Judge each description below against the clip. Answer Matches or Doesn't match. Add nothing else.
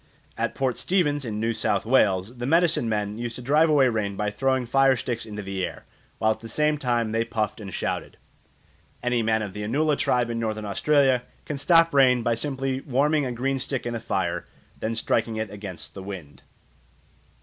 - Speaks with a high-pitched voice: Doesn't match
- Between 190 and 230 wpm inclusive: Matches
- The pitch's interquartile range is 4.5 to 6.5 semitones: Doesn't match